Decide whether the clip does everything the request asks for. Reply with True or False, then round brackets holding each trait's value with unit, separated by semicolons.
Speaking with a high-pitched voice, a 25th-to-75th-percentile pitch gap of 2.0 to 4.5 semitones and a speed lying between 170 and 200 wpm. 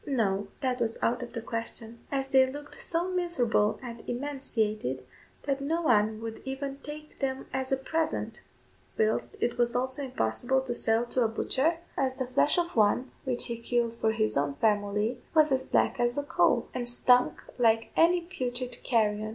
True (245 Hz; 3.3 semitones; 180 wpm)